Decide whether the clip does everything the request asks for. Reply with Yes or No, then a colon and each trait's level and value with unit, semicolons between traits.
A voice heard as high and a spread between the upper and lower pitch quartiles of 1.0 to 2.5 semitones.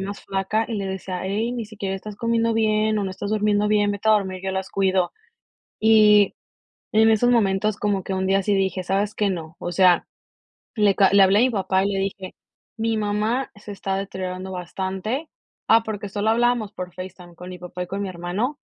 Yes: high, 200 Hz; narrow, 2.2 semitones